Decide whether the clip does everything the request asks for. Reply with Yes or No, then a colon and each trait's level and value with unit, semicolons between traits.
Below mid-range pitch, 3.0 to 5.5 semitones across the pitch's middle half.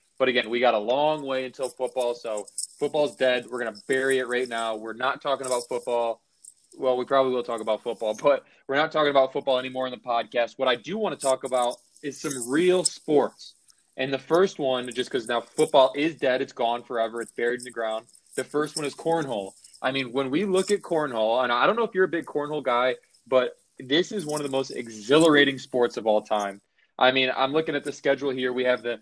Yes: low, 130 Hz; average, 3.4 semitones